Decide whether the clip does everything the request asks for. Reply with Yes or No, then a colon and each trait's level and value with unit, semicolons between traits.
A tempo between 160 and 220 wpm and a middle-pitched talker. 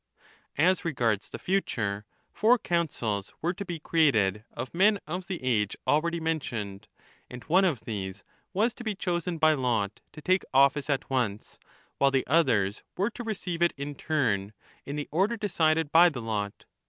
Yes: average, 175 wpm; medium, 150 Hz